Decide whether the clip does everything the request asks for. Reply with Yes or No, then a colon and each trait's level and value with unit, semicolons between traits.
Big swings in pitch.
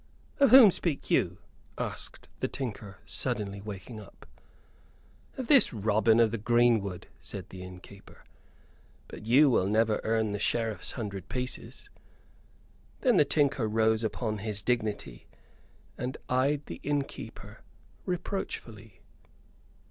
No: average, 4.2 semitones